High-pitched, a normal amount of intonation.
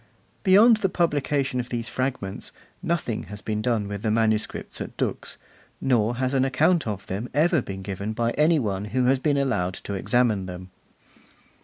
No: low, 120 Hz; average, 5.0 semitones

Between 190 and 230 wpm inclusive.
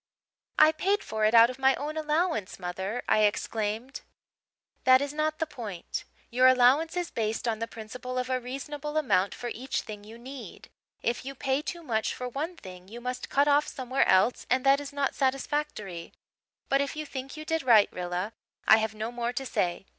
Yes: average, 200 wpm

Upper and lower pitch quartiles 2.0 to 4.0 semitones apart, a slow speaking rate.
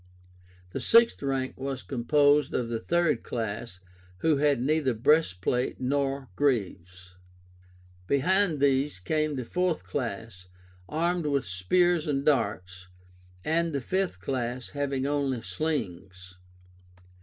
No: average, 5.1 semitones; slow, 115 wpm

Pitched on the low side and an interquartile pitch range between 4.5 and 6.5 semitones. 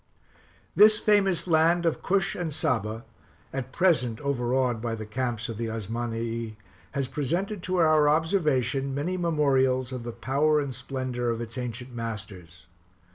Yes: low, 130 Hz; average, 5.2 semitones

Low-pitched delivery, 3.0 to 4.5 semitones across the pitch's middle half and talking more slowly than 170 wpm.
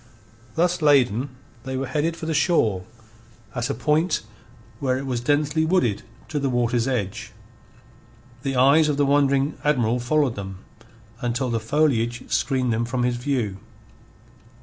Yes: low, 130 Hz; average, 3.6 semitones; average, 150 wpm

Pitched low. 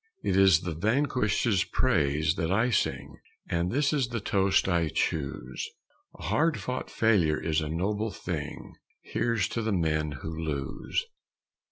Yes: very low, 95 Hz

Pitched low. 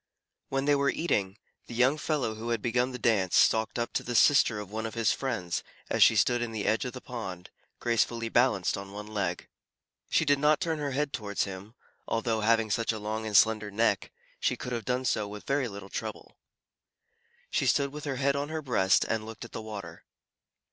Yes: low, 115 Hz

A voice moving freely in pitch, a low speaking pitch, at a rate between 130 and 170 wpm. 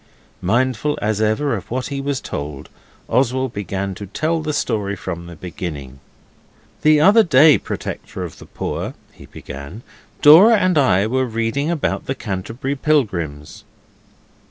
Yes: wide, 7.3 semitones; low, 120 Hz; average, 145 wpm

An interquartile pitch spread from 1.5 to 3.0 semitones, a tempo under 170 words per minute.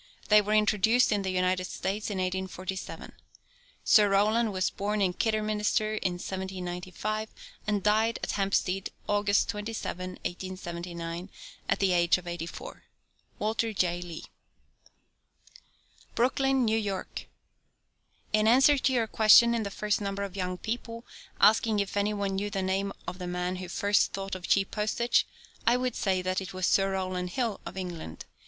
Yes: average, 2.7 semitones; average, 160 wpm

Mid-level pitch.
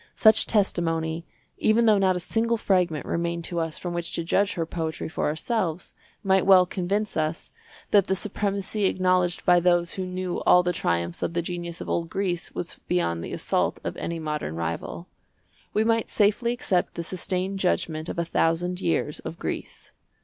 Yes: medium, 175 Hz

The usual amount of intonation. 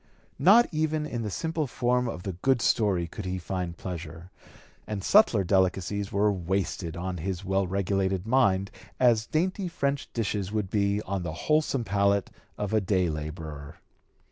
Yes: average, 4.6 semitones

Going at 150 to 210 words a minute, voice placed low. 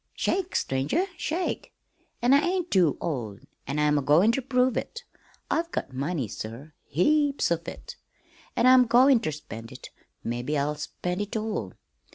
No: average, 160 wpm; medium, 180 Hz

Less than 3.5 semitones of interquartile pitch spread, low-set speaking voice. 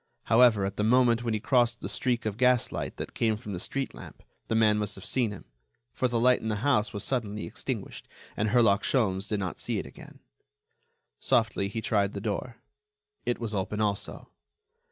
Yes: average, 2.9 semitones; low, 110 Hz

